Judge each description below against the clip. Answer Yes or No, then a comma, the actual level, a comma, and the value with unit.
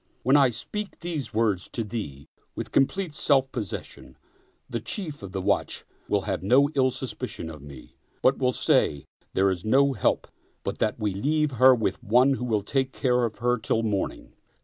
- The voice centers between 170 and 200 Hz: No, low, 125 Hz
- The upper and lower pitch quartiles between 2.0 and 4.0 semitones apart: No, average, 5.0 semitones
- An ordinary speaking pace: Yes, average, 180 wpm